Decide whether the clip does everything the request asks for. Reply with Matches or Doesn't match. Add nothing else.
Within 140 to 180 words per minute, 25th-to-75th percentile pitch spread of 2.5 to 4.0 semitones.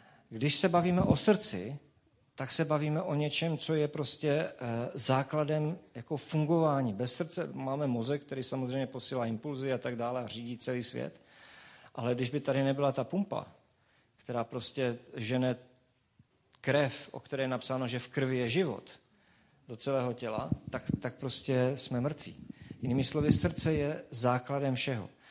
Matches